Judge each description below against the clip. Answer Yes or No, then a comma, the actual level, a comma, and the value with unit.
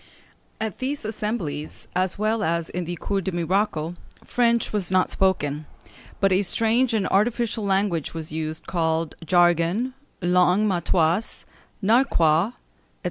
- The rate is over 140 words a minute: No, slow, 135 wpm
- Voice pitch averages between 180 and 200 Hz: Yes, medium, 185 Hz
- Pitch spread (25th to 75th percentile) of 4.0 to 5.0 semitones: Yes, average, 4.4 semitones